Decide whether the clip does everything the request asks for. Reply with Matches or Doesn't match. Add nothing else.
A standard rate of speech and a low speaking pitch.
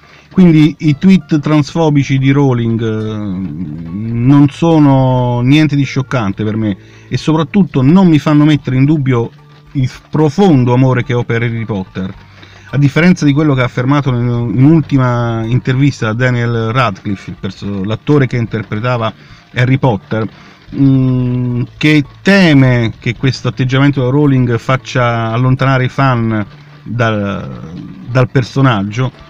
Matches